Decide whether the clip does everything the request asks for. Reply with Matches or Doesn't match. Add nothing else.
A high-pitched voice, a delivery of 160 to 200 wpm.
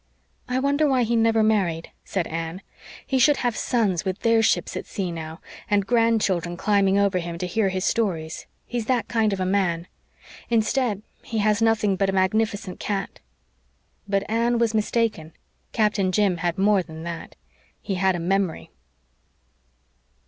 Matches